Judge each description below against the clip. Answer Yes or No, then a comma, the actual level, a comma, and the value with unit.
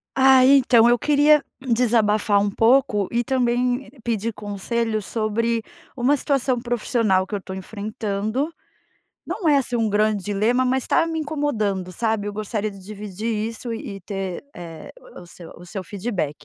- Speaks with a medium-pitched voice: No, high, 225 Hz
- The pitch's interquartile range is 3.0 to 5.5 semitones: Yes, average, 3.6 semitones